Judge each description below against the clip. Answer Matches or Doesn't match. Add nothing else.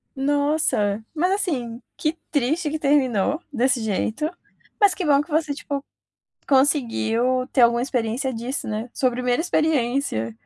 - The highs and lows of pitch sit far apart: Doesn't match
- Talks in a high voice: Matches